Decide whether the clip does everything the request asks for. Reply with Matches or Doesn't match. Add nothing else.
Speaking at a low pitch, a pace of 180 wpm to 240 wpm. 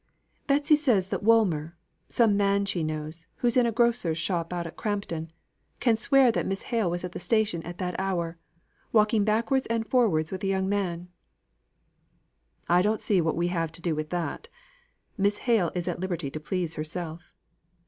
Doesn't match